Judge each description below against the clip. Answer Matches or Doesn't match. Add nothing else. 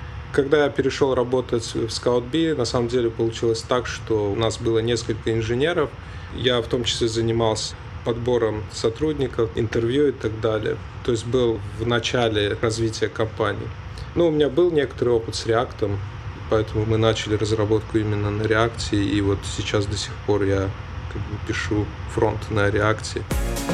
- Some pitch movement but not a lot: Doesn't match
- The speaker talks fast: Matches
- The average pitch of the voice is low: Matches